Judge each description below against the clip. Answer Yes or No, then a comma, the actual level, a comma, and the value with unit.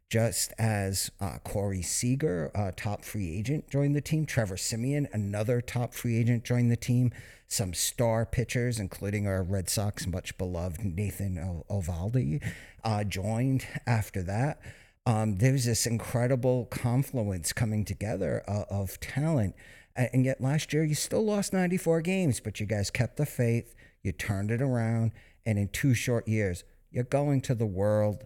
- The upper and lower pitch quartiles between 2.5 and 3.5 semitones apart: No, average, 4.2 semitones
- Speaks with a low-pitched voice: Yes, low, 115 Hz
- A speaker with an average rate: Yes, average, 160 wpm